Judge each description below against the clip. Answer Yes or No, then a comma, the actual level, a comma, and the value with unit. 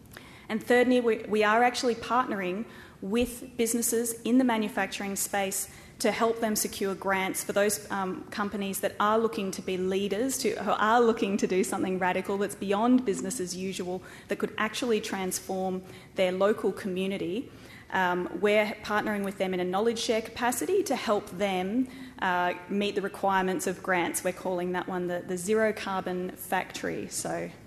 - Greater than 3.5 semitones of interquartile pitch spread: No, average, 3.1 semitones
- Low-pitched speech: No, high, 205 Hz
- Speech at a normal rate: Yes, average, 165 wpm